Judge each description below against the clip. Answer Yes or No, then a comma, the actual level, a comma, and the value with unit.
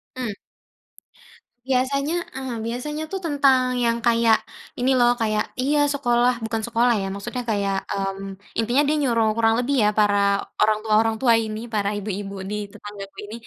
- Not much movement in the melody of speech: No, average, 3.3 semitones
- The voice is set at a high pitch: Yes, high, 230 Hz